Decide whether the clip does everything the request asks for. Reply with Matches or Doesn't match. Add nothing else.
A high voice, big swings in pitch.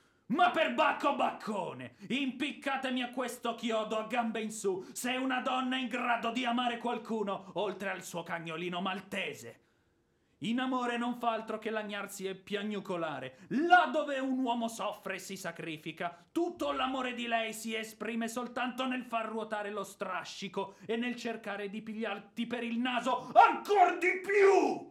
Doesn't match